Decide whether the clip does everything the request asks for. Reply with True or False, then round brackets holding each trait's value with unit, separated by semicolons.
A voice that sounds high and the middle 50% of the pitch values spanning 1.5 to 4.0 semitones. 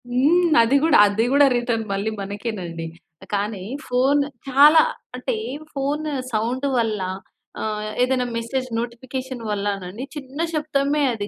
False (245 Hz; 4.7 semitones)